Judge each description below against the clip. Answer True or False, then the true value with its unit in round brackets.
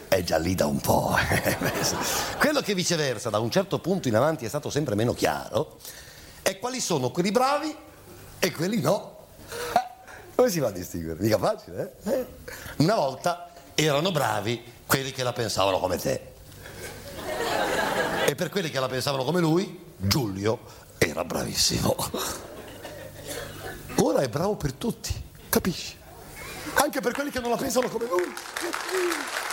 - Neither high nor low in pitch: True (170 Hz)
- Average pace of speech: True (150 wpm)